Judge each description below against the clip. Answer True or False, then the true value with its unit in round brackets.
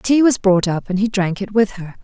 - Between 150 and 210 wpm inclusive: False (295 wpm)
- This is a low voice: False (205 Hz)